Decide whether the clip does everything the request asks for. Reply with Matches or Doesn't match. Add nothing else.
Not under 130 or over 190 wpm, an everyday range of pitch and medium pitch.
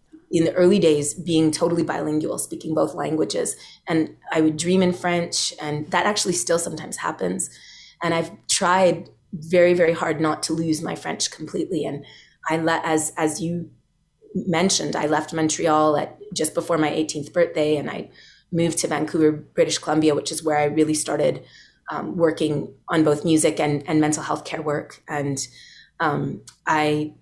Doesn't match